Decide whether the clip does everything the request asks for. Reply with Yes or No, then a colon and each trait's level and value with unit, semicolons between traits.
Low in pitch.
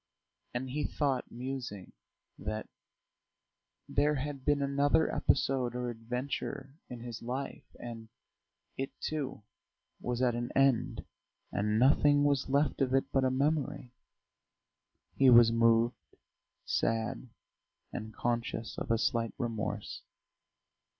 Yes: low, 125 Hz